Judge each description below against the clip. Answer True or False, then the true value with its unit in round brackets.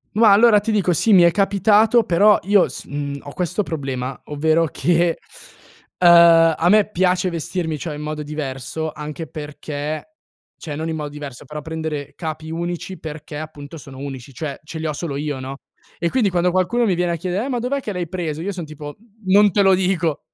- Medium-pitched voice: True (165 Hz)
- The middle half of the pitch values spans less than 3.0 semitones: False (3.8 semitones)